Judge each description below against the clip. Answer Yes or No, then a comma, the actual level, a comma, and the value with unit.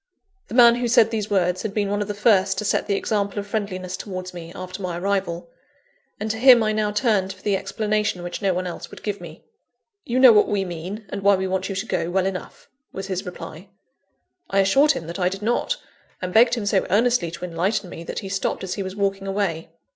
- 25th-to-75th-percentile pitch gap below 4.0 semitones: Yes, narrow, 2.5 semitones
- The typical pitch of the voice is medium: No, high, 195 Hz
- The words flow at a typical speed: No, fast, 240 wpm